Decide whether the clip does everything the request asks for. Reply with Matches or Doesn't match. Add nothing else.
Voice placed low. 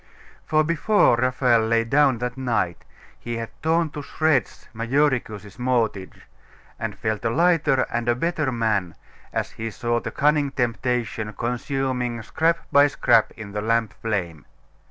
Matches